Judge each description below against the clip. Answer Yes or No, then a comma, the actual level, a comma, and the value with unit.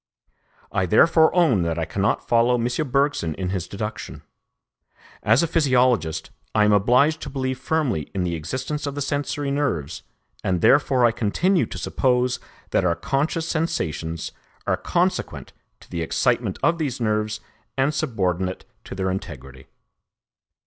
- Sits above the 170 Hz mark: No, low, 120 Hz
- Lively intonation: Yes, wide, 7.5 semitones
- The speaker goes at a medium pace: Yes, average, 150 wpm